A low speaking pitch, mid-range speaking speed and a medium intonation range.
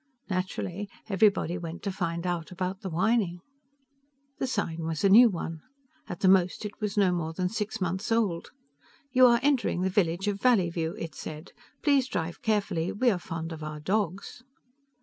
No: medium, 185 Hz; average, 175 wpm; average, 3.8 semitones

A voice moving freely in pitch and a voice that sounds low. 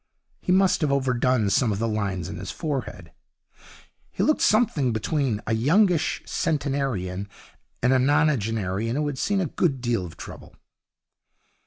Yes: wide, 5.8 semitones; low, 130 Hz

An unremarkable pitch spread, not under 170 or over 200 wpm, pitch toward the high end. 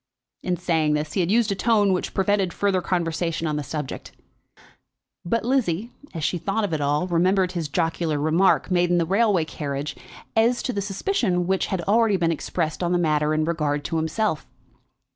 No: average, 4.0 semitones; average, 190 wpm; medium, 175 Hz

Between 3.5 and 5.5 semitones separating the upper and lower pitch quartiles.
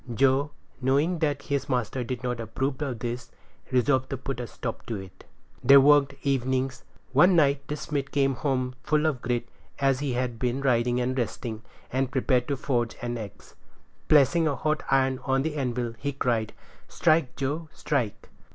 No: narrow, 2.4 semitones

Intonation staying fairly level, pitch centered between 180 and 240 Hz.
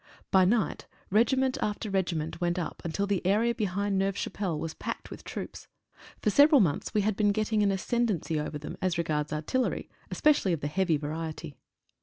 No: average, 4.6 semitones; high, 190 Hz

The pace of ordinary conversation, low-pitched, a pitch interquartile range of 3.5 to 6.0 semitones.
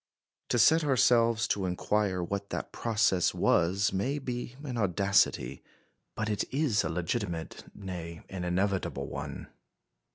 No: slow, 130 wpm; low, 100 Hz; average, 4.6 semitones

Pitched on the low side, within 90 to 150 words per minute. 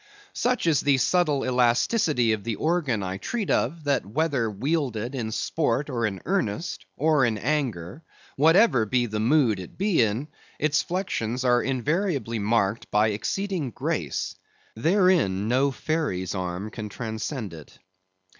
Yes: low, 125 Hz; average, 145 wpm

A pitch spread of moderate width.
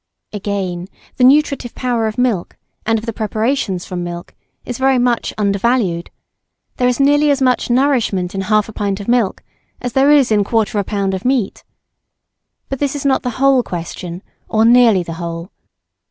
Yes: average, 4.7 semitones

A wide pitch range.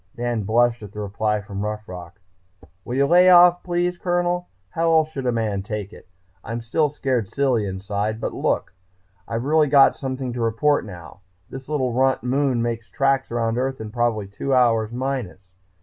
No: average, 4.4 semitones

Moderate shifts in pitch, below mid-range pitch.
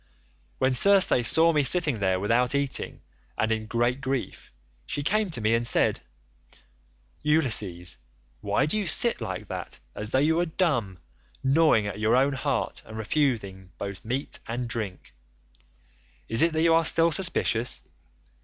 No: wide, 6.4 semitones; low, 125 Hz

